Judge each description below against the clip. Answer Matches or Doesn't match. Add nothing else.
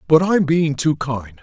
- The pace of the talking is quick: Matches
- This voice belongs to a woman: Doesn't match